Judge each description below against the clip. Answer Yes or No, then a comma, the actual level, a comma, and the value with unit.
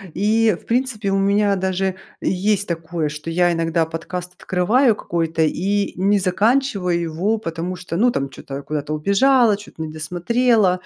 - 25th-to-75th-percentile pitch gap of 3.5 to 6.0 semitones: Yes, average, 4.0 semitones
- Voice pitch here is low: No, medium, 185 Hz